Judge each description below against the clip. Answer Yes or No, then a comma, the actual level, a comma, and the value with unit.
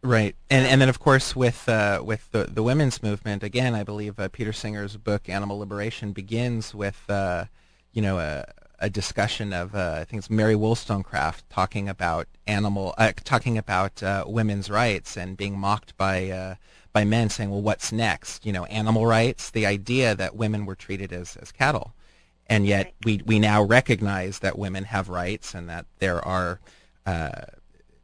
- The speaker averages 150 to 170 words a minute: No, average, 180 wpm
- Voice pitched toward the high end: No, low, 105 Hz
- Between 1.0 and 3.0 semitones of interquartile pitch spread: Yes, narrow, 2.6 semitones